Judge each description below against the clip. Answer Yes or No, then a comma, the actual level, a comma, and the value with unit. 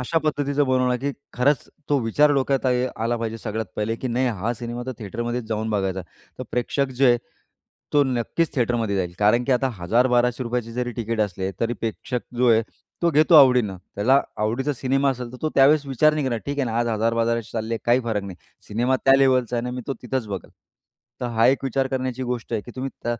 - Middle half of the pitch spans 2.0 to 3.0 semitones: Yes, average, 2.7 semitones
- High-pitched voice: No, low, 125 Hz